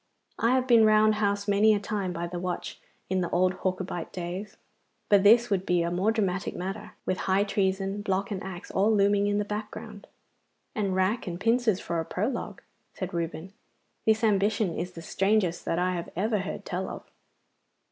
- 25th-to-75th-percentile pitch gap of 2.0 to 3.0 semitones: Yes, narrow, 2.6 semitones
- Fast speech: No, average, 190 wpm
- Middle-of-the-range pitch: No, high, 195 Hz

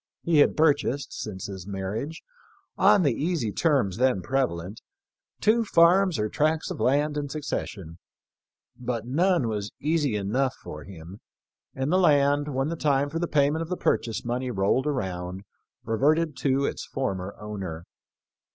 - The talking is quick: No, average, 150 wpm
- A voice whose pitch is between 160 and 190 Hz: No, low, 135 Hz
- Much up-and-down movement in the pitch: Yes, wide, 6.9 semitones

